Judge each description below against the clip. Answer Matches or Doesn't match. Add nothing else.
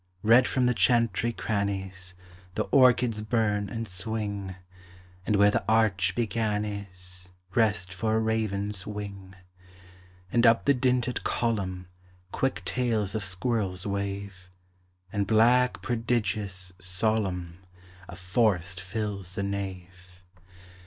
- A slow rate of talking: Matches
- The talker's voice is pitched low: Matches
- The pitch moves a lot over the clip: Doesn't match